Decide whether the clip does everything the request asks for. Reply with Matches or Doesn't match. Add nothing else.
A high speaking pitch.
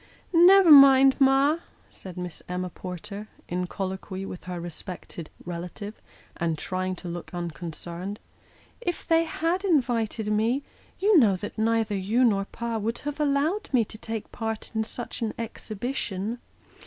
Matches